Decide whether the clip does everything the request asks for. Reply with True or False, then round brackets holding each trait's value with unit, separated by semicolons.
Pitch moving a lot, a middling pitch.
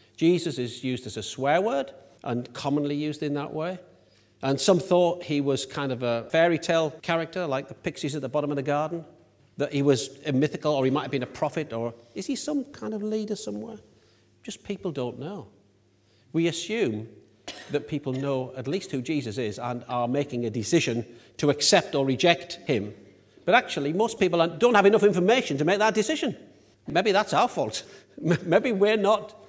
True (5.7 semitones; 145 Hz)